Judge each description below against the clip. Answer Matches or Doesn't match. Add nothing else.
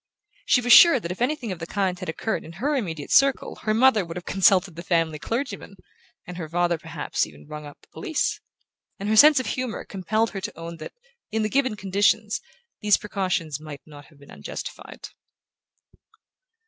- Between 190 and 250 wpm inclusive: Matches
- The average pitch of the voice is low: Doesn't match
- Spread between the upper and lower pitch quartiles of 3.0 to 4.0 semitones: Doesn't match